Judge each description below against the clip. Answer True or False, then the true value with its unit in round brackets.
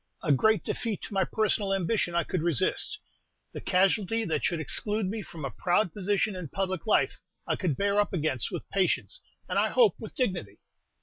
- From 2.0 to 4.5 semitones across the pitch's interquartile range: True (3.5 semitones)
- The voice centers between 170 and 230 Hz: True (190 Hz)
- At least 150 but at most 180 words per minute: False (190 wpm)